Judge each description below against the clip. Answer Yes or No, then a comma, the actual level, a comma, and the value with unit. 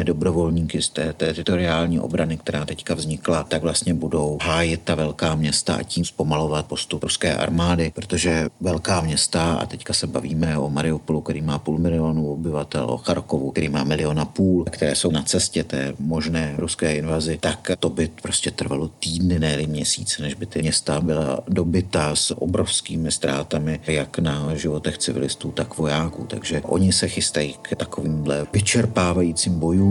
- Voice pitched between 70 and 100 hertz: Yes, very low, 80 Hz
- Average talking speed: Yes, average, 160 wpm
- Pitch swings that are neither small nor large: No, narrow, 2.1 semitones